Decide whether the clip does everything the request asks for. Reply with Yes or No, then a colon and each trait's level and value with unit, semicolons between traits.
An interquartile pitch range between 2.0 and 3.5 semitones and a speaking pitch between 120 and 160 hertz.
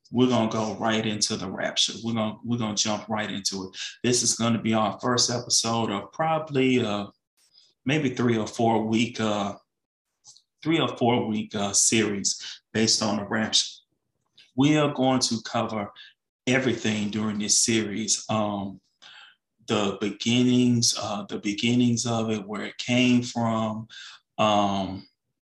No: narrow, 2.4 semitones; low, 110 Hz